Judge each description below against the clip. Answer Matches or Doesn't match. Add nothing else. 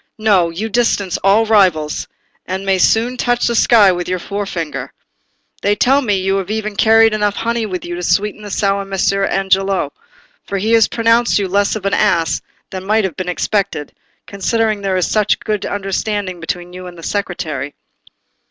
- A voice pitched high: Matches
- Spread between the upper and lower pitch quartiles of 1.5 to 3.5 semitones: Matches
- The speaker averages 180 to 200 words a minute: Matches